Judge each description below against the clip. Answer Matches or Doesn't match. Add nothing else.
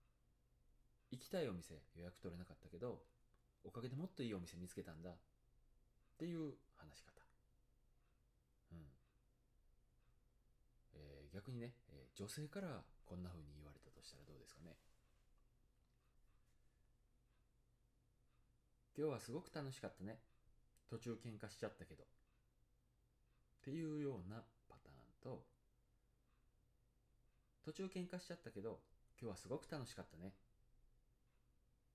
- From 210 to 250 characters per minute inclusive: Matches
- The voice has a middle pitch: Doesn't match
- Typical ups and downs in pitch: Doesn't match